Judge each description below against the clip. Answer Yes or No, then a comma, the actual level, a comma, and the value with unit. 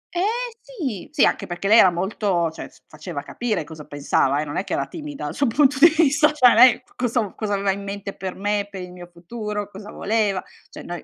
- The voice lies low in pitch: No, high, 205 Hz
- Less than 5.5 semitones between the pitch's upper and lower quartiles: No, wide, 6.3 semitones